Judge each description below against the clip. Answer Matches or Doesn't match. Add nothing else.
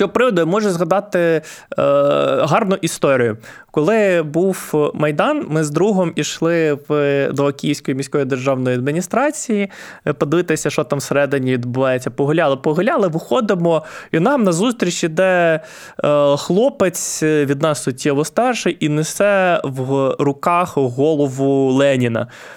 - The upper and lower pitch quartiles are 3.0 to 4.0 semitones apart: Doesn't match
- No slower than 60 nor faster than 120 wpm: Matches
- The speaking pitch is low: Doesn't match